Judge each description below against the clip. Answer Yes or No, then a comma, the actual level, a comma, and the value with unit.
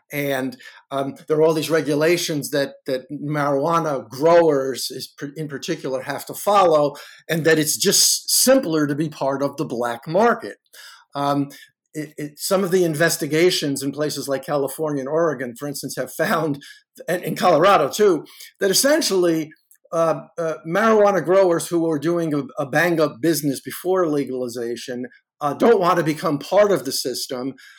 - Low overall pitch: No, medium, 155 Hz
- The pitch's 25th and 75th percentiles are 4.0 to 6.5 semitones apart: No, average, 3.4 semitones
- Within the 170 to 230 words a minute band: No, average, 160 wpm